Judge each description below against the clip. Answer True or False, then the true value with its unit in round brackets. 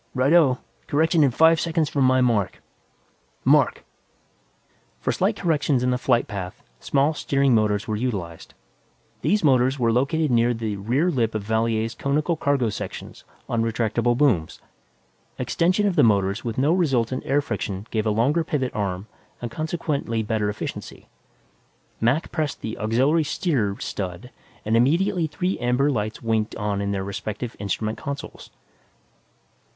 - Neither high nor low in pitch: False (125 Hz)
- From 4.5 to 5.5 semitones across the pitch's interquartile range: True (5.1 semitones)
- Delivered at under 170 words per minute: True (150 wpm)